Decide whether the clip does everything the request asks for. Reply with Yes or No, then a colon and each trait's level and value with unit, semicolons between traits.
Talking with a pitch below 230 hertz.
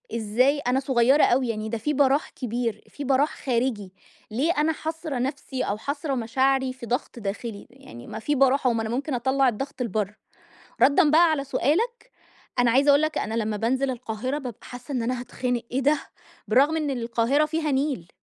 No: very high, 260 Hz